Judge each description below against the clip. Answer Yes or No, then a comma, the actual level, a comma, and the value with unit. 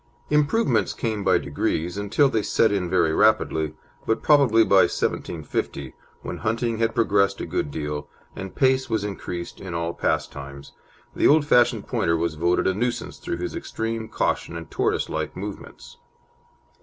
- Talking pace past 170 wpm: No, average, 155 wpm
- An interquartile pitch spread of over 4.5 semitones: Yes, average, 5.2 semitones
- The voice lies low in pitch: Yes, low, 100 Hz